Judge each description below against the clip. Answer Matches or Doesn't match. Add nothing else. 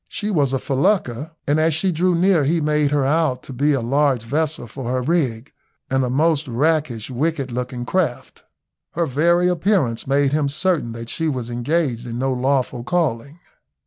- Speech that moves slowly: Doesn't match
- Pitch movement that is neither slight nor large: Matches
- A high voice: Doesn't match